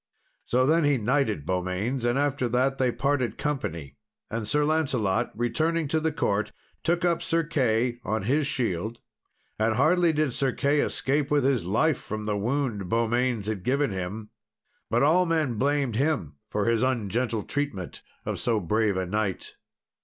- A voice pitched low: Yes, low, 125 Hz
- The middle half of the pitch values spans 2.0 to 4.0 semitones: No, average, 5.2 semitones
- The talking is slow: No, average, 165 wpm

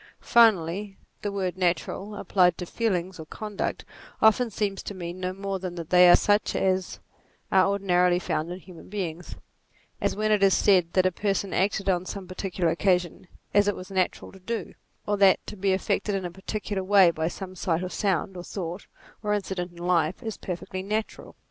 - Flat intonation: Yes, narrow, 2.2 semitones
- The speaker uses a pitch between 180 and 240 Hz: Yes, high, 190 Hz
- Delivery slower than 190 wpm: No, average, 195 wpm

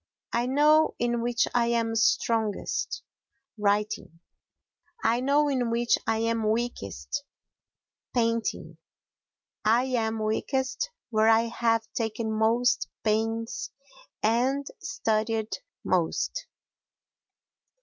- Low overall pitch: No, high, 230 Hz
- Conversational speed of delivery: No, slow, 90 wpm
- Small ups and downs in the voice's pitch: Yes, narrow, 1.8 semitones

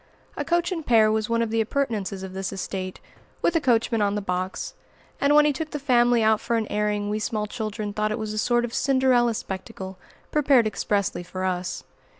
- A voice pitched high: Yes, high, 220 Hz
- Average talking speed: No, fast, 210 wpm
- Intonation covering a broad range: No, average, 3.2 semitones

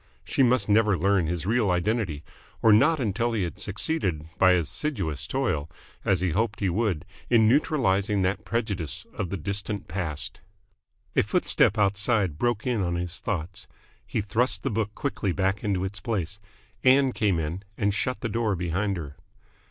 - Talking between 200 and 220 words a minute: No, average, 165 wpm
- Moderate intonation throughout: Yes, average, 3.9 semitones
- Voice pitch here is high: No, low, 100 Hz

